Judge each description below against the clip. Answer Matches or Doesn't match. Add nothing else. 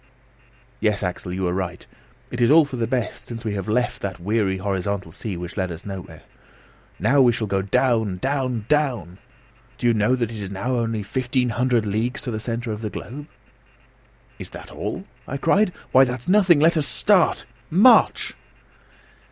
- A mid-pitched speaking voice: Doesn't match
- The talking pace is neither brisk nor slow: Matches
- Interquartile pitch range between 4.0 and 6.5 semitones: Matches